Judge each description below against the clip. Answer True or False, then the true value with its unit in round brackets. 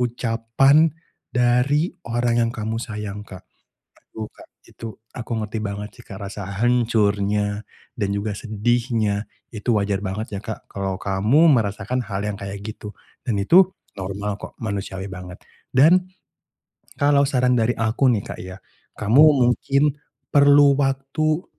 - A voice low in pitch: True (110 Hz)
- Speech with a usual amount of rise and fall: True (3.9 semitones)